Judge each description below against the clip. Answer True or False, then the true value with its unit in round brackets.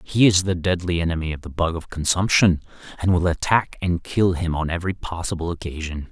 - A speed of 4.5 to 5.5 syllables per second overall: False (5.7 syllables/s)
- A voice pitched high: False (85 Hz)